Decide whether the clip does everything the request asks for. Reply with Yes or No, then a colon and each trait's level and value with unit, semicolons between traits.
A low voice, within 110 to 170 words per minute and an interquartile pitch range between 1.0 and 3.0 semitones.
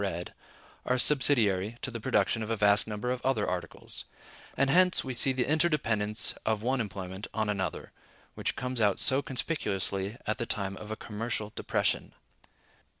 No: low, 110 Hz; average, 165 wpm; average, 3.9 semitones